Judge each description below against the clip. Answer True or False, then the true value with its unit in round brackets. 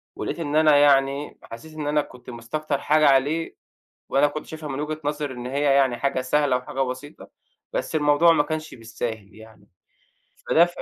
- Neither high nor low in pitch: True (145 Hz)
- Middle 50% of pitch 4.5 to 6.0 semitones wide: False (3.1 semitones)